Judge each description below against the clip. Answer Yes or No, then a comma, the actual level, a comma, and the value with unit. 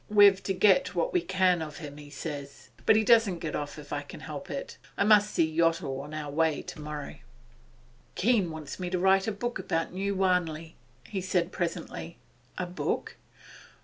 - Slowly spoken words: No, average, 185 wpm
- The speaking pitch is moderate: Yes, medium, 175 Hz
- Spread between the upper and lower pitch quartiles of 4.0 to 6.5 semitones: Yes, average, 4.5 semitones